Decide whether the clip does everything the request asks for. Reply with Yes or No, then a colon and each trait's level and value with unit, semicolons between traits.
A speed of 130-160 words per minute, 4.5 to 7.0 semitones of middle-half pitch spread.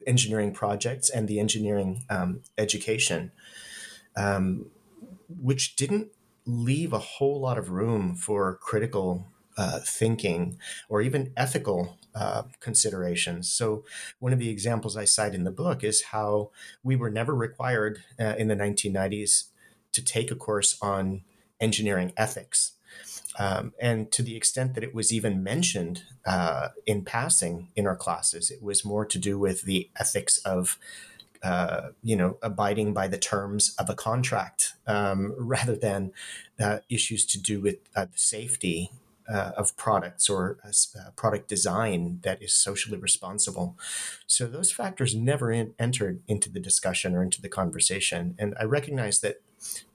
No: average, 150 wpm; average, 3.2 semitones